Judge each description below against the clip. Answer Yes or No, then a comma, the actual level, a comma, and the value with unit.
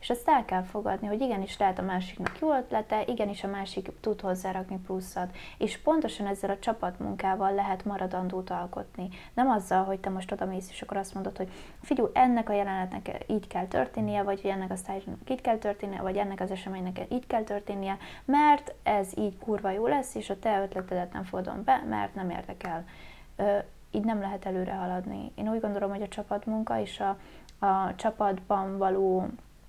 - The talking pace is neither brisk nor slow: No, fast, 180 wpm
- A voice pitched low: No, high, 195 Hz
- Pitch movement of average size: No, narrow, 2.2 semitones